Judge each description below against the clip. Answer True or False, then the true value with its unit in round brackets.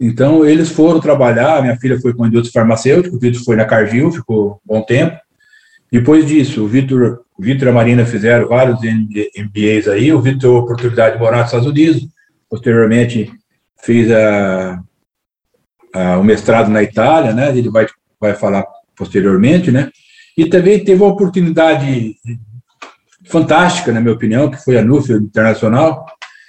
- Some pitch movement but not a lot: False (5.7 semitones)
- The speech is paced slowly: False (160 wpm)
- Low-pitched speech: True (120 Hz)